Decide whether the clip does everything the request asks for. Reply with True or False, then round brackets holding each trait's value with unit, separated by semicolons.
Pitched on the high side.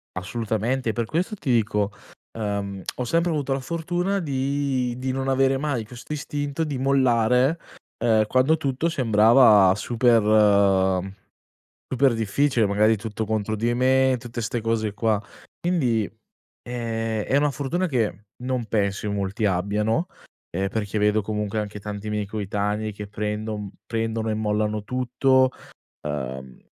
False (115 Hz)